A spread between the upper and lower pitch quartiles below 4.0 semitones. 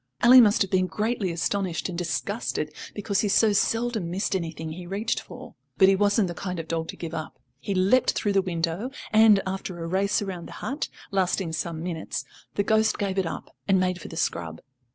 Yes: average, 3.3 semitones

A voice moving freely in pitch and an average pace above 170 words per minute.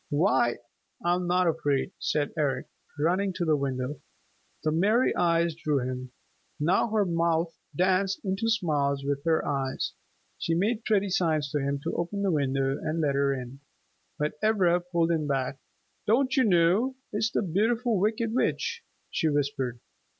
No: wide, 5.7 semitones; average, 155 wpm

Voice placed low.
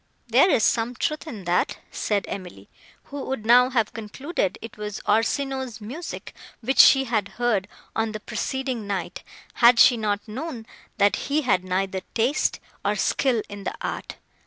No: high, 225 Hz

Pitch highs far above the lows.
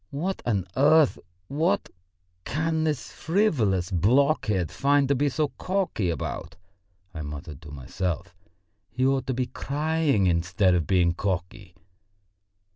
Yes: wide, 8.8 semitones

